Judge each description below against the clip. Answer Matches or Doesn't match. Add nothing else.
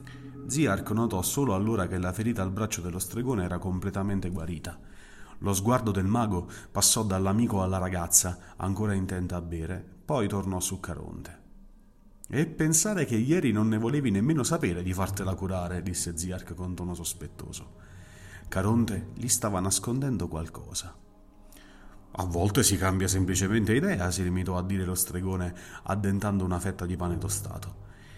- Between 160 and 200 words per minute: Doesn't match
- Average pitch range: Matches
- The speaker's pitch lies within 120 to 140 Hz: Doesn't match